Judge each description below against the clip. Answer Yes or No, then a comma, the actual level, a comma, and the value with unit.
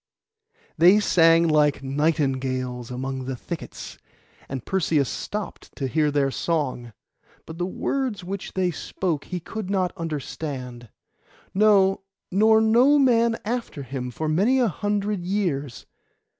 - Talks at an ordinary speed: No, slow, 130 wpm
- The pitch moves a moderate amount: No, wide, 6.8 semitones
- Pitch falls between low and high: Yes, medium, 165 Hz